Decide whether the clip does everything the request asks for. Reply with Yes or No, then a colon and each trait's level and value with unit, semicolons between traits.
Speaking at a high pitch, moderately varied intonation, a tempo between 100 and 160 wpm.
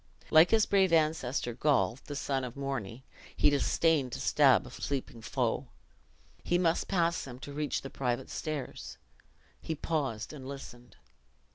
No: medium, 140 Hz; average, 3.9 semitones; average, 150 wpm